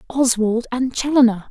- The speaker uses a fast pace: No, slow, 120 wpm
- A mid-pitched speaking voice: No, high, 240 Hz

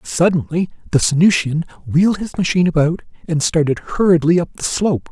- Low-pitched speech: No, medium, 165 Hz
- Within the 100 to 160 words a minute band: Yes, average, 150 wpm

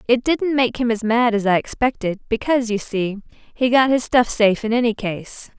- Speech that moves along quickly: Yes, fast, 215 wpm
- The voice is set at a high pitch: Yes, high, 230 Hz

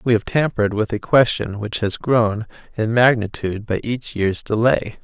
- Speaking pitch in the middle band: No, low, 110 Hz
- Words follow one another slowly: No, average, 180 wpm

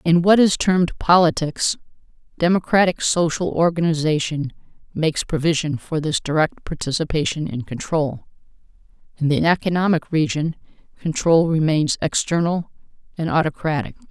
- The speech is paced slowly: Yes, slow, 105 wpm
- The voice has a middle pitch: Yes, medium, 165 Hz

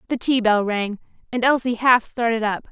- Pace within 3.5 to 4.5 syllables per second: No, 5.0 syllables/s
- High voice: Yes, high, 230 Hz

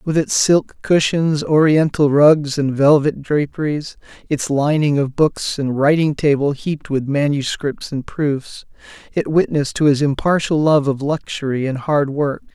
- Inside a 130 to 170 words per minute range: Yes, average, 155 wpm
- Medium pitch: Yes, medium, 145 Hz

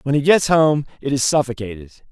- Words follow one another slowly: No, average, 200 wpm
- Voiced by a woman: No, male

